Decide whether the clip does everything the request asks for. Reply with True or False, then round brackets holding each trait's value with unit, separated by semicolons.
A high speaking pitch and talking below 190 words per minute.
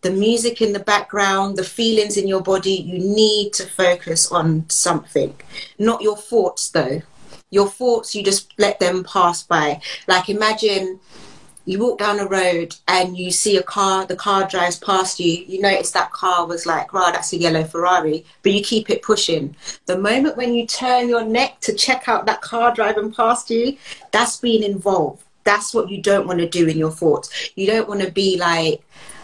False (195 Hz; 195 wpm)